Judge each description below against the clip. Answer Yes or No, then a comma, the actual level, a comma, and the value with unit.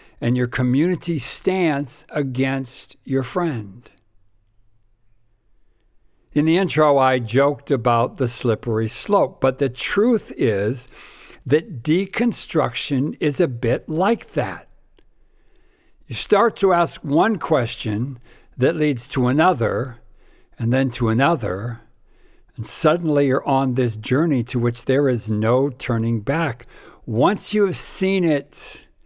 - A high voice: No, low, 135 Hz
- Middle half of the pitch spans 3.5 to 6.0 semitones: Yes, average, 5.0 semitones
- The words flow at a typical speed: No, slow, 120 wpm